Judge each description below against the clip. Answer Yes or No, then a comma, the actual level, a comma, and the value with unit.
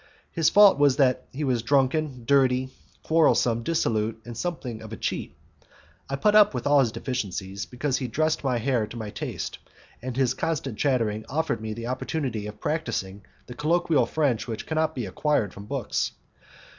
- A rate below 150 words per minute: No, average, 175 wpm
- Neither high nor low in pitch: No, low, 130 Hz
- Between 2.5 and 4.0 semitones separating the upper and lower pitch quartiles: No, average, 5.0 semitones